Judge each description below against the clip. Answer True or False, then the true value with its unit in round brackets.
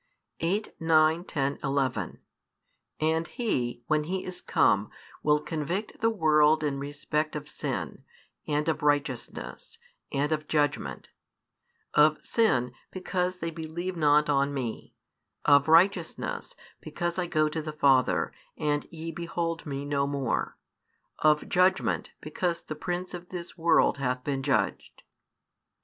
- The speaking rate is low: True (130 wpm)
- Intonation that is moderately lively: True (3.0 semitones)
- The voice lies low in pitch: False (155 Hz)